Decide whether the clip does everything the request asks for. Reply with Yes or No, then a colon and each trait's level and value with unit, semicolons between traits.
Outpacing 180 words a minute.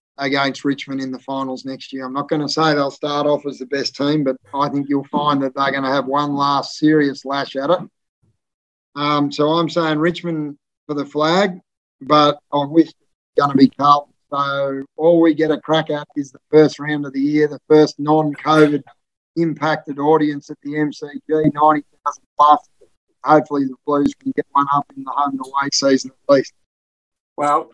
Yes: average, 195 wpm